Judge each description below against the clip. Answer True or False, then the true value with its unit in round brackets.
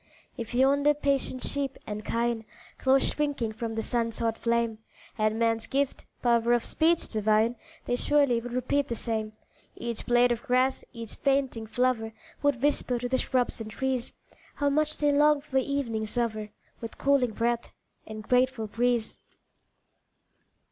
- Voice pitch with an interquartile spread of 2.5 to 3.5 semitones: True (3.1 semitones)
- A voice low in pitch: False (240 Hz)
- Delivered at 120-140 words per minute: False (155 wpm)